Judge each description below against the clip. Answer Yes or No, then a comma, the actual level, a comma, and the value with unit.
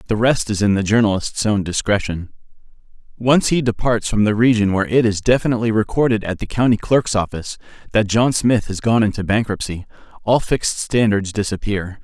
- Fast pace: No, average, 175 wpm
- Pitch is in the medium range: No, low, 110 Hz